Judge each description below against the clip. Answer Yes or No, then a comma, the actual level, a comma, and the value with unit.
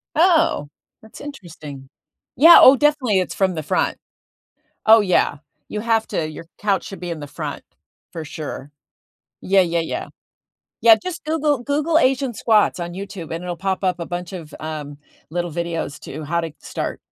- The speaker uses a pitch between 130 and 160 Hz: No, medium, 185 Hz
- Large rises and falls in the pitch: Yes, wide, 6.2 semitones